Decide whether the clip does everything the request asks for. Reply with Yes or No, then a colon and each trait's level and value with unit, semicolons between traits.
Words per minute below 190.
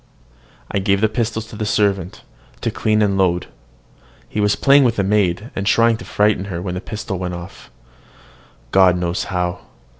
Yes: average, 180 wpm